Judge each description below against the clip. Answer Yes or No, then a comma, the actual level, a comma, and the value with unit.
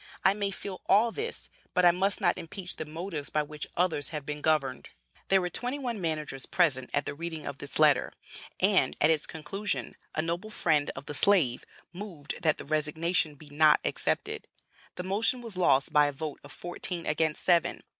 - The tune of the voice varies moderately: Yes, average, 3.8 semitones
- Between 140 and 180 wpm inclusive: No, average, 195 wpm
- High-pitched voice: No, medium, 160 Hz